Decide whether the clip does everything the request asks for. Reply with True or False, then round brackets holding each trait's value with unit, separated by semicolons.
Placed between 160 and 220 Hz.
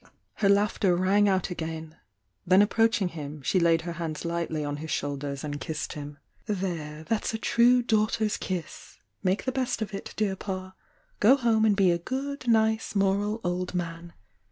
True (185 Hz)